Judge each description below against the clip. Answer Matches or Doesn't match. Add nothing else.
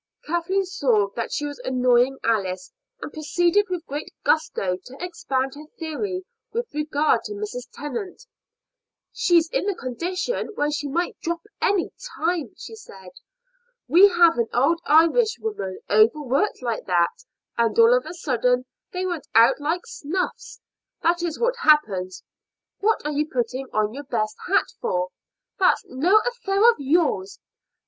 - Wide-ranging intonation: Matches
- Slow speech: Doesn't match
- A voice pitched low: Doesn't match